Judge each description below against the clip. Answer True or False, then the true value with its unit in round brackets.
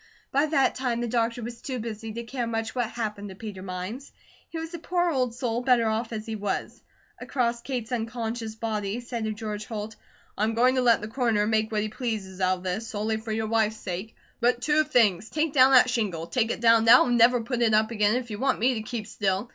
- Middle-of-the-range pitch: False (230 Hz)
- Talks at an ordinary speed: False (240 wpm)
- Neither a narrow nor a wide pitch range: False (2.3 semitones)